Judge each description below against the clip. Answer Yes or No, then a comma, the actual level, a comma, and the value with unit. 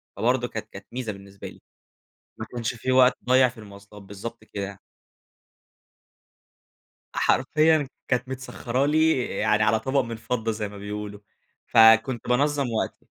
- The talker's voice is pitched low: Yes, low, 115 Hz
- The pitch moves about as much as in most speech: Yes, average, 3.6 semitones